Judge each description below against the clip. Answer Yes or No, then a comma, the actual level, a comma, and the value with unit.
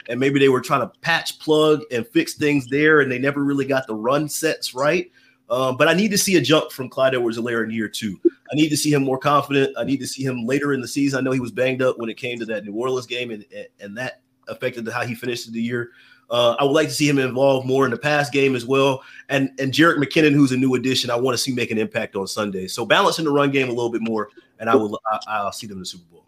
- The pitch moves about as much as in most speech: Yes, average, 3.2 semitones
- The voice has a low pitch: Yes, low, 130 Hz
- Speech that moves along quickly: Yes, fast, 290 wpm